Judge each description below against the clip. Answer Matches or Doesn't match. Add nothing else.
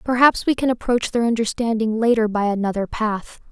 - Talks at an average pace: Matches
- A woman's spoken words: Matches